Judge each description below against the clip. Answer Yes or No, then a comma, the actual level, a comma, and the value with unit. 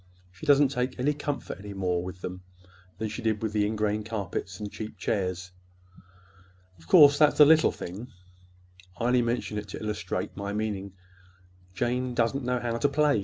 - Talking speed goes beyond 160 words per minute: Yes, average, 170 wpm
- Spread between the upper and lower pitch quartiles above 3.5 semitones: Yes, average, 4.0 semitones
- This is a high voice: No, low, 110 Hz